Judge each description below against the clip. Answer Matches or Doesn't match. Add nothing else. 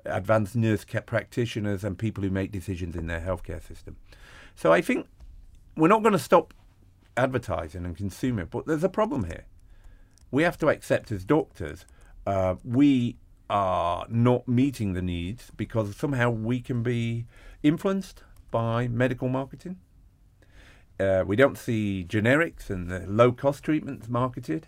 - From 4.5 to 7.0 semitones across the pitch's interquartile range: Matches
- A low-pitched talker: Matches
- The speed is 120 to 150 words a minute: Matches